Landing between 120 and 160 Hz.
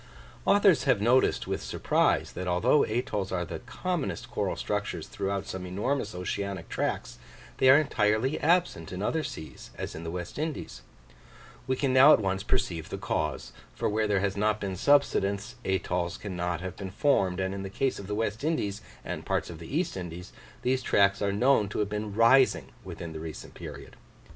No: low, 100 Hz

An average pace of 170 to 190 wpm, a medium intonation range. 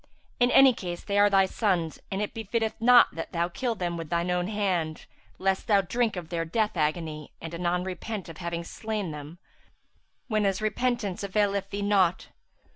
Yes: average, 180 wpm; average, 3.8 semitones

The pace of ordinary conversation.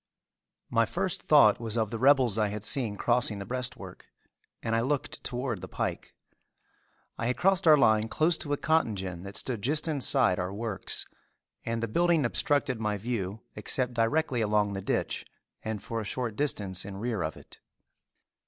Yes: average, 180 wpm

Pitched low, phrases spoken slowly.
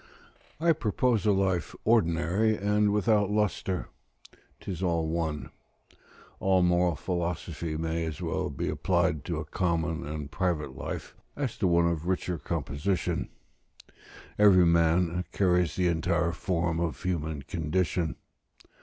Yes: very low, 85 Hz; slow, 125 wpm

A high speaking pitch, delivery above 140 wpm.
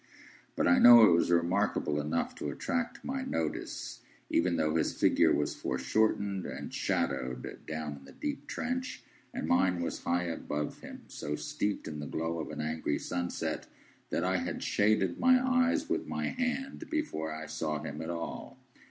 No: very low, 85 Hz; average, 170 wpm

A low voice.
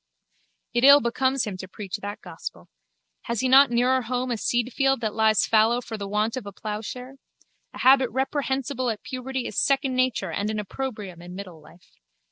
No: high, 240 Hz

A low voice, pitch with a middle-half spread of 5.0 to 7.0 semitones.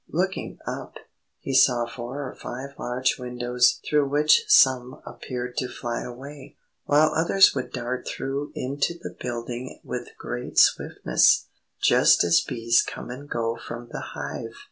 No: low, 125 Hz; narrow, 2.6 semitones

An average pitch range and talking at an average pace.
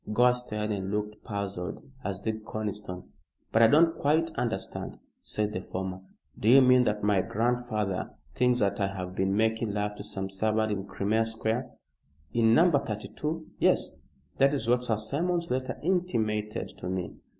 Yes: average, 3.5 semitones; average, 165 wpm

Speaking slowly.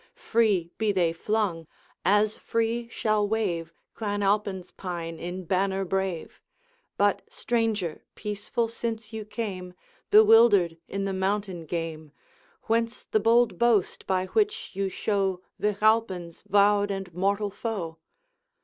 Yes: slow, 125 wpm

